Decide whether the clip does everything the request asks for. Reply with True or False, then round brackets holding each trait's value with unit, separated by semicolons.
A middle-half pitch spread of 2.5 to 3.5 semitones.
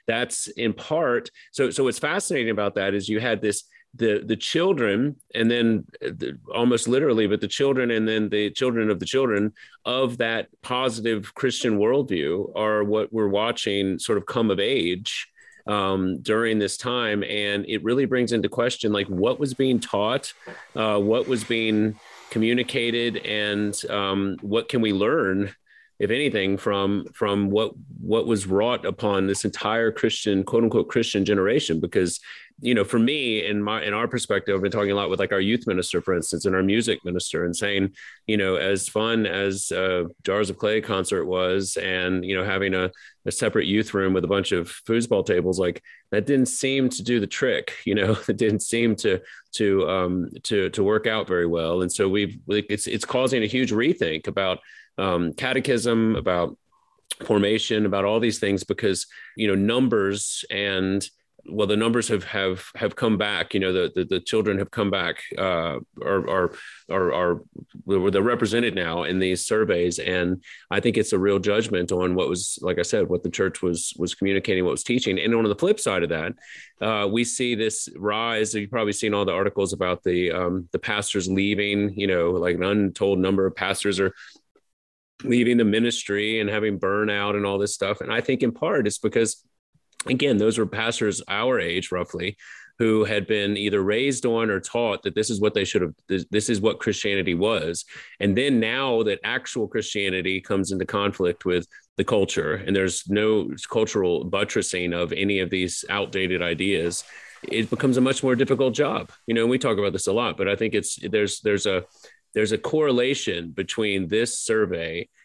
True (2.8 semitones)